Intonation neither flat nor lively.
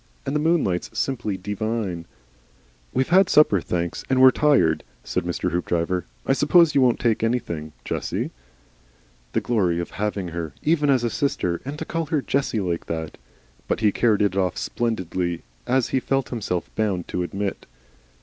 No: wide, 7.1 semitones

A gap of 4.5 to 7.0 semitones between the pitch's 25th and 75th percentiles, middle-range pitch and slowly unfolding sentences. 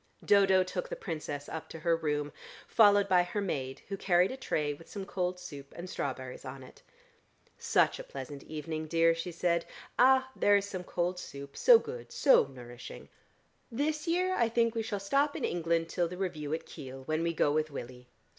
No: wide, 5.4 semitones; medium, 175 Hz; average, 195 wpm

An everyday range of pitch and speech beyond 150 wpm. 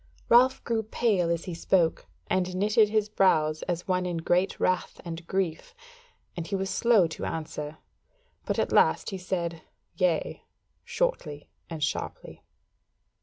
No: average, 4.0 semitones; average, 145 wpm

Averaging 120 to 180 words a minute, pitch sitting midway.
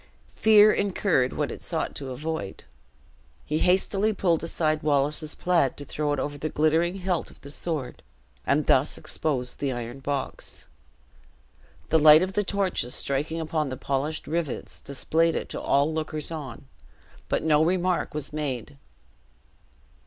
Yes: average, 150 wpm; medium, 155 Hz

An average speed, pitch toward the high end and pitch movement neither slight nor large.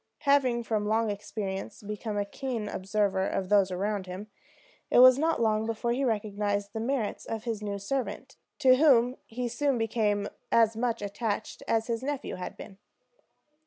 Yes: average, 165 wpm; high, 220 Hz; average, 3.1 semitones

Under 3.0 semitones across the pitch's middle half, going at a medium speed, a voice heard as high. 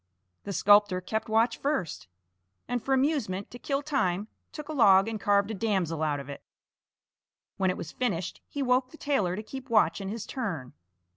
No: wide, 5.5 semitones; average, 190 wpm; high, 210 Hz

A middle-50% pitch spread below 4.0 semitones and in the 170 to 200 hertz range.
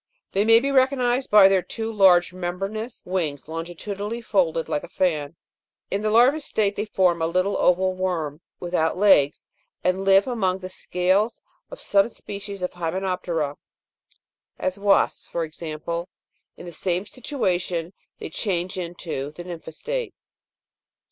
Yes: average, 3.2 semitones; medium, 185 Hz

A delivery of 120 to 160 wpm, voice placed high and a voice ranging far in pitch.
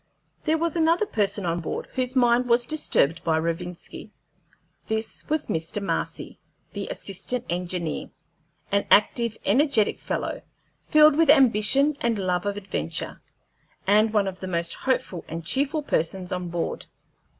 Yes: average, 140 wpm; high, 210 Hz; wide, 6.9 semitones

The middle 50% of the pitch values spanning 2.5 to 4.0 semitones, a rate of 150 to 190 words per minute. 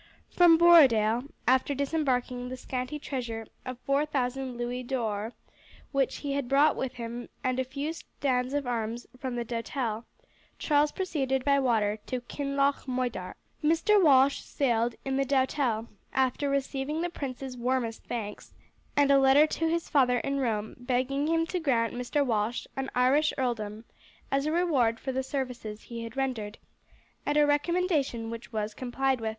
Yes: average, 2.9 semitones; average, 160 wpm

